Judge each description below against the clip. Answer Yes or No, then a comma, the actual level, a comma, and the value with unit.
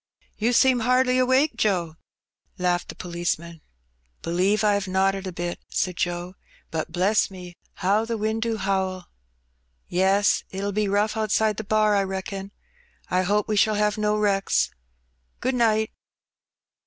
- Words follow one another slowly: No, average, 155 wpm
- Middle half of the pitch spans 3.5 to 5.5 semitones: No, average, 3.0 semitones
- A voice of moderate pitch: No, high, 200 Hz